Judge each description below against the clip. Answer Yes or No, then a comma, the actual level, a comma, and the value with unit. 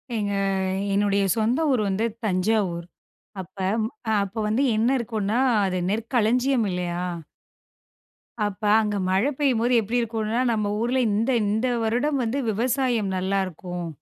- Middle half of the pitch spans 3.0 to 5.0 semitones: Yes, average, 3.3 semitones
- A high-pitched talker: Yes, high, 220 Hz